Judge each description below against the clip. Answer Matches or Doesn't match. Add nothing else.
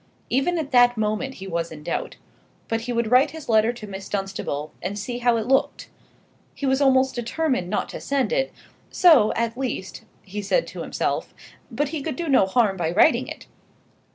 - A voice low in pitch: Doesn't match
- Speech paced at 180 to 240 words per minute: Matches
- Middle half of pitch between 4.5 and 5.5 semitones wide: Matches